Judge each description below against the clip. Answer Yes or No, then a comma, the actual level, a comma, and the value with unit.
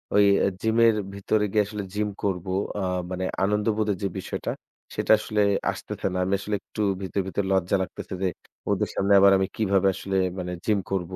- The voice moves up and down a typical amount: No, narrow, 1.8 semitones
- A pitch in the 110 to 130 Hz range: No, low, 100 Hz